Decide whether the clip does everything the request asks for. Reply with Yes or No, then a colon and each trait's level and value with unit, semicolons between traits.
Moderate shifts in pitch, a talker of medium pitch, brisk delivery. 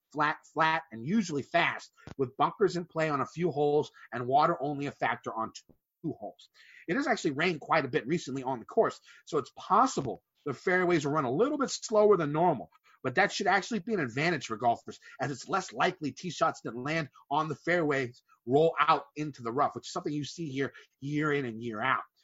Yes: average, 4.2 semitones; medium, 150 Hz; fast, 220 wpm